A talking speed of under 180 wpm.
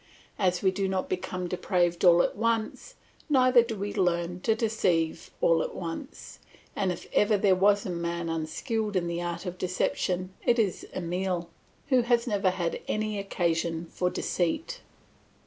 Yes: average, 165 wpm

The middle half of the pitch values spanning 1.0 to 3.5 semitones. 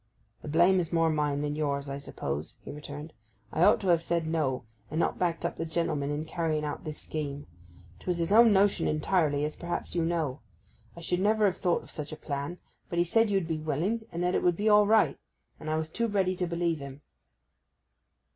Yes: average, 3.2 semitones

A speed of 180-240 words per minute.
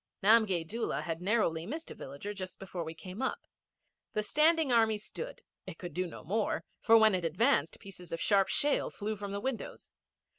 Yes: average, 190 wpm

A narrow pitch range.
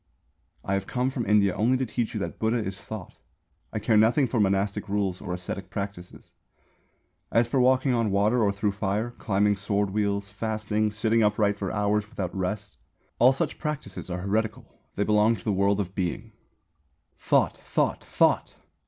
Yes: narrow, 2.1 semitones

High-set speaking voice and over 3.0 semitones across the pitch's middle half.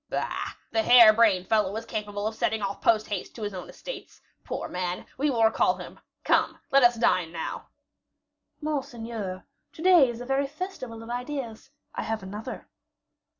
Yes: high, 225 Hz; average, 3.4 semitones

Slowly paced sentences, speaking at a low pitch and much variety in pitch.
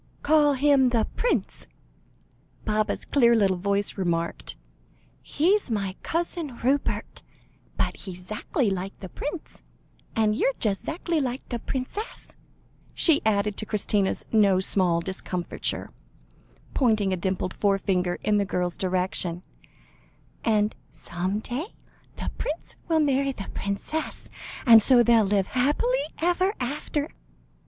No: slow, 125 wpm; high, 215 Hz; wide, 6.5 semitones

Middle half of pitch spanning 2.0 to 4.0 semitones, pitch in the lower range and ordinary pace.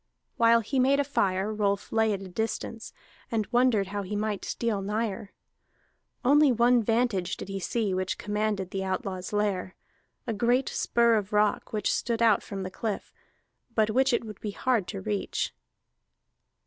No: average, 3.0 semitones; high, 215 Hz; average, 170 wpm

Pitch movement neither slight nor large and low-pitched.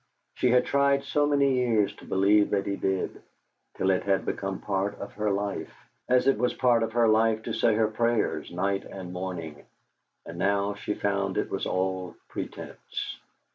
Yes: average, 3.3 semitones; low, 100 Hz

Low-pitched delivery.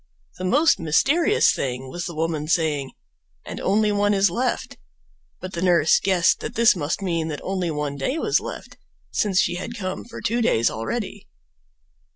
No: medium, 185 Hz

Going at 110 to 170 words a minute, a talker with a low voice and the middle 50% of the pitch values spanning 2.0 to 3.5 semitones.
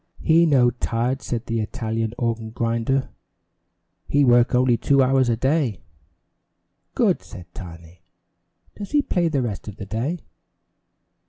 Yes: average, 140 wpm; low, 120 Hz; average, 3.2 semitones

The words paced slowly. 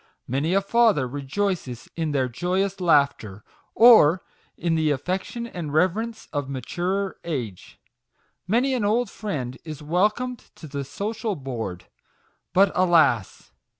Yes: slow, 125 wpm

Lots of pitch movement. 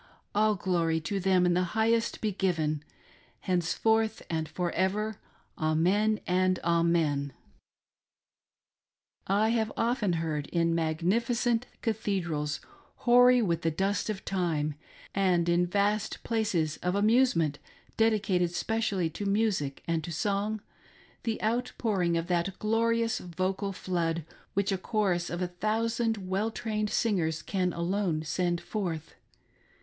No: average, 4.2 semitones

